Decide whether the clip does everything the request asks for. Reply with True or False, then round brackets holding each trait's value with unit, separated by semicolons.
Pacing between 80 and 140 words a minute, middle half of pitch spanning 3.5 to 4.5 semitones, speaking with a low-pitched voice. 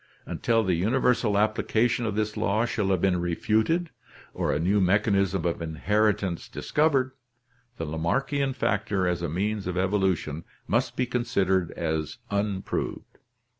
True (135 wpm; 4.0 semitones; 100 Hz)